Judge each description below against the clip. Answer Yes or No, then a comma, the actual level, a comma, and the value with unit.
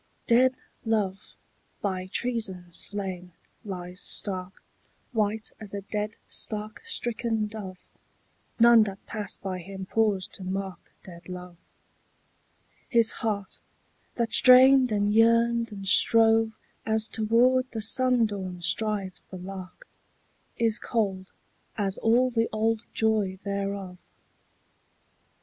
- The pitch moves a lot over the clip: No, average, 3.1 semitones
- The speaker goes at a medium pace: No, slow, 110 wpm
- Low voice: No, high, 210 Hz